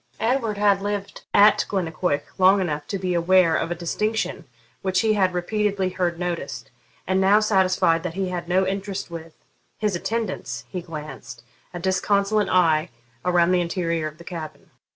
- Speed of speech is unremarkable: Yes, average, 165 wpm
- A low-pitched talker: No, medium, 185 Hz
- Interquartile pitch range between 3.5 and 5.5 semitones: No, average, 2.8 semitones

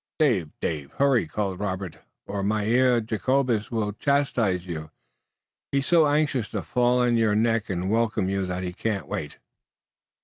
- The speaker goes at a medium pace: Yes, average, 150 wpm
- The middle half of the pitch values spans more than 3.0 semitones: Yes, average, 4.7 semitones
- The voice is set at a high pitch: No, low, 110 Hz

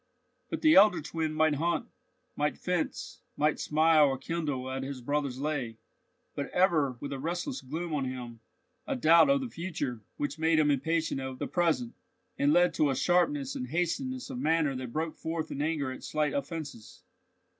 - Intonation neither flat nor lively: Yes, average, 3.6 semitones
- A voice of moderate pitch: Yes, medium, 155 Hz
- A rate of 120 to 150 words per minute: No, average, 180 wpm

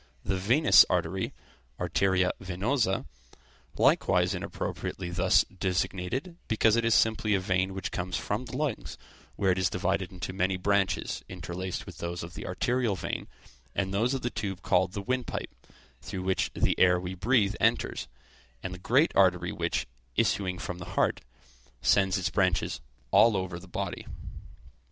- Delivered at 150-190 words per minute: Yes, average, 155 wpm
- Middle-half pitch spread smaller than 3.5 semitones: Yes, average, 2.9 semitones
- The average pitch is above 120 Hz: No, very low, 95 Hz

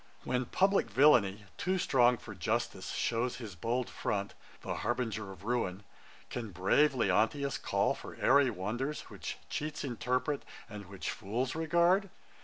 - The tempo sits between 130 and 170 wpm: Yes, average, 140 wpm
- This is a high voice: No, low, 120 Hz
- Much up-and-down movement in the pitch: Yes, wide, 5.7 semitones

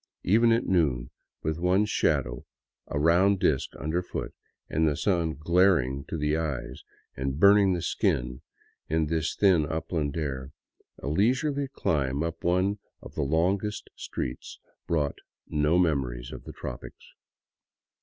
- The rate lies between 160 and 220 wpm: No, average, 140 wpm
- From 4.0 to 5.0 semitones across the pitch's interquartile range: Yes, average, 4.7 semitones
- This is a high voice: No, very low, 80 Hz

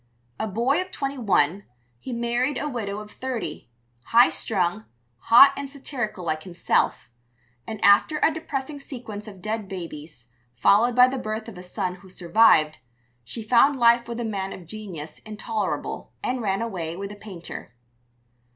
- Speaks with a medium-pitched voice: No, high, 215 Hz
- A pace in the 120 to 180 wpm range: Yes, average, 160 wpm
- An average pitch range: Yes, average, 4.9 semitones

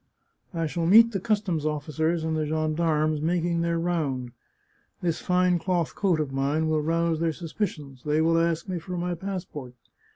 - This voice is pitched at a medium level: Yes, medium, 165 Hz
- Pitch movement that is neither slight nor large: No, narrow, 2.3 semitones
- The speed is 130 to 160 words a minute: No, average, 175 wpm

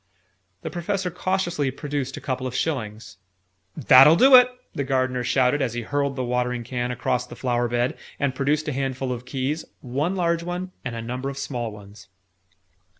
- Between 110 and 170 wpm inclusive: No, average, 180 wpm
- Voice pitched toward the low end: Yes, low, 130 Hz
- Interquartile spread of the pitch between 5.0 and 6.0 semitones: No, average, 3.4 semitones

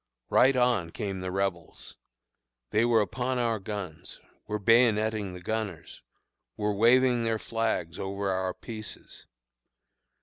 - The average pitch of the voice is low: Yes, low, 105 Hz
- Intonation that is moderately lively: Yes, average, 3.2 semitones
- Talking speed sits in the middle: No, slow, 125 wpm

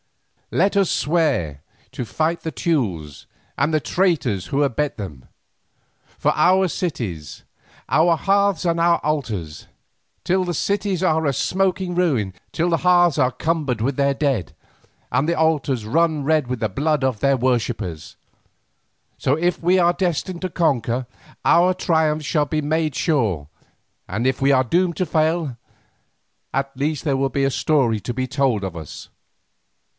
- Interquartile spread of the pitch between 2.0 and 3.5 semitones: No, average, 5.3 semitones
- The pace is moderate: Yes, average, 160 wpm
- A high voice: No, medium, 150 Hz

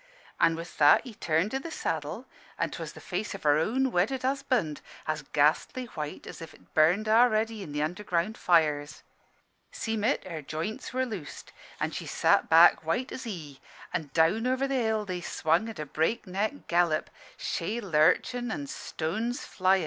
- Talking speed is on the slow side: No, average, 175 wpm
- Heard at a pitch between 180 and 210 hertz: Yes, medium, 185 Hz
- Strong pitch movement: Yes, wide, 6.4 semitones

